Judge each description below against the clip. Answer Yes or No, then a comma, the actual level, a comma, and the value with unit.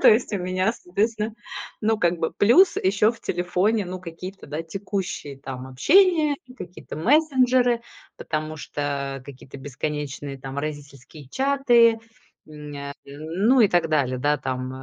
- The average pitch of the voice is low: No, medium, 175 Hz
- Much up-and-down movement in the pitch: Yes, wide, 7.8 semitones